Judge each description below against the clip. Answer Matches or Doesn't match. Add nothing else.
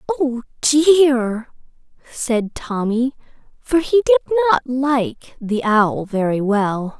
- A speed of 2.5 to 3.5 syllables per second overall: Matches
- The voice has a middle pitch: Doesn't match